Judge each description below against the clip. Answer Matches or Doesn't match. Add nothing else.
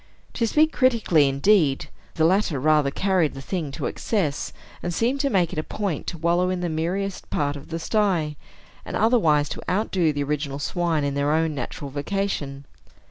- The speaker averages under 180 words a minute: Doesn't match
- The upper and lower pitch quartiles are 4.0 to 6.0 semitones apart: Matches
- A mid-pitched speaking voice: Matches